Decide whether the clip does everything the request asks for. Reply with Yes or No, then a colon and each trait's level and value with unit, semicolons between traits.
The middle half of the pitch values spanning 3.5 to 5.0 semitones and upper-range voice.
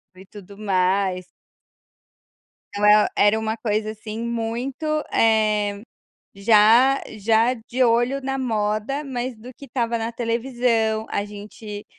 No: narrow, 2.5 semitones; high, 220 Hz